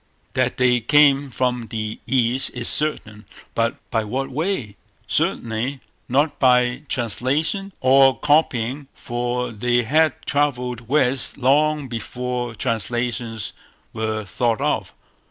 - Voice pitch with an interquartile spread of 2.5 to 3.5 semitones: Yes, average, 2.9 semitones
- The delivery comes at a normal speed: No, slow, 115 wpm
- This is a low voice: Yes, low, 125 Hz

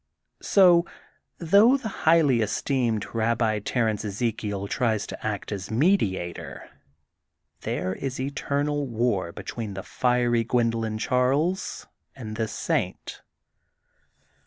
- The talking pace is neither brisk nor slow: No, slow, 110 wpm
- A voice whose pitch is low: Yes, low, 115 Hz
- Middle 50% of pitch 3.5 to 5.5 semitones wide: Yes, average, 4.6 semitones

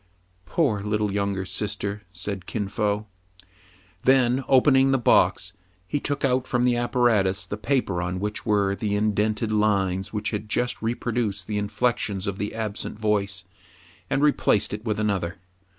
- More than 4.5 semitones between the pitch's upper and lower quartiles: No, average, 3.2 semitones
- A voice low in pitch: Yes, low, 105 Hz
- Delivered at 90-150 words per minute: No, average, 160 wpm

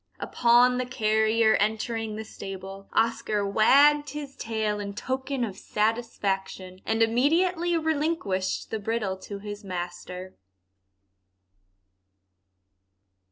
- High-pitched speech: Yes, high, 220 Hz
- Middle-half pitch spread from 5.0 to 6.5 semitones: No, average, 4.1 semitones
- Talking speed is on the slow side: Yes, slow, 100 wpm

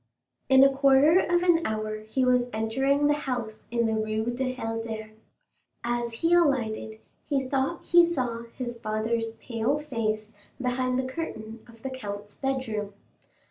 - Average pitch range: Yes, average, 3.5 semitones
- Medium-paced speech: Yes, average, 150 wpm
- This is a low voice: No, high, 240 Hz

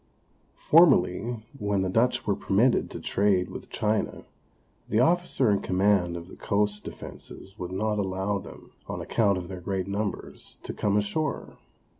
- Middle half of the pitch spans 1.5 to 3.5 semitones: Yes, narrow, 2.4 semitones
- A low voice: Yes, low, 100 Hz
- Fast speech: No, average, 155 wpm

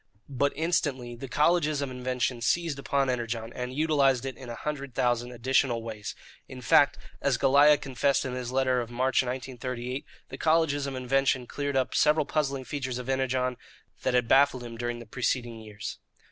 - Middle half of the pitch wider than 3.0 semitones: No, narrow, 2.4 semitones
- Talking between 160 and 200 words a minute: Yes, average, 175 wpm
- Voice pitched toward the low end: Yes, low, 130 Hz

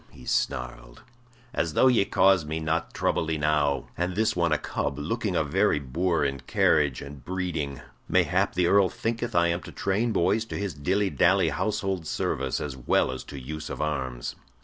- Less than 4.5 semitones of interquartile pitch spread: No, average, 4.9 semitones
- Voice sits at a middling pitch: No, very low, 80 Hz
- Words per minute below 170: No, average, 185 wpm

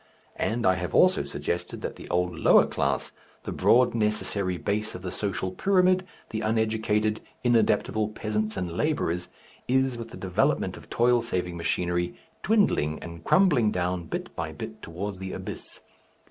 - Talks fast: No, average, 155 wpm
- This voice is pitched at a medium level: No, low, 105 Hz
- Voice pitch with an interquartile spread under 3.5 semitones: No, average, 4.5 semitones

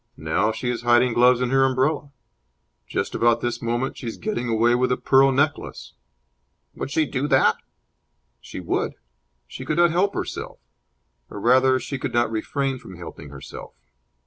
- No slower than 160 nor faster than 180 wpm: Yes, average, 170 wpm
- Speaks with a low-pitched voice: Yes, low, 125 Hz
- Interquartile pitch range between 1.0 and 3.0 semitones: Yes, narrow, 2.4 semitones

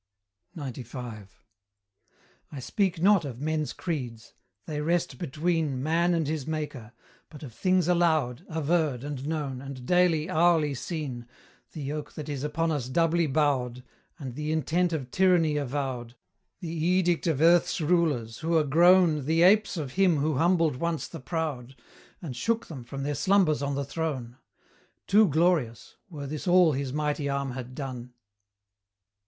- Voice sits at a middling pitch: Yes, medium, 150 Hz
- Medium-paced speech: Yes, average, 155 wpm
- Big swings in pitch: No, average, 4.0 semitones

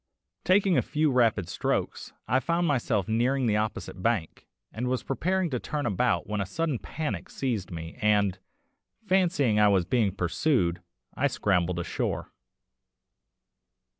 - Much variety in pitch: Yes, wide, 6.7 semitones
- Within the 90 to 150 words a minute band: Yes, average, 140 wpm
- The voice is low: Yes, low, 115 Hz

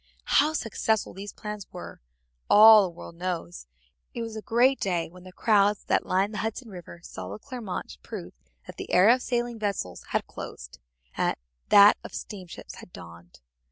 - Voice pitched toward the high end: Yes, high, 200 Hz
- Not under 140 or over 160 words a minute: No, average, 175 wpm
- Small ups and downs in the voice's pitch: No, average, 4.1 semitones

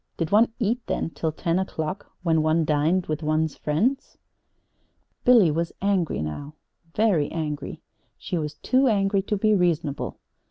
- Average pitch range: Yes, average, 4.6 semitones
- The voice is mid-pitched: Yes, medium, 170 Hz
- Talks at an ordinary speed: Yes, average, 150 wpm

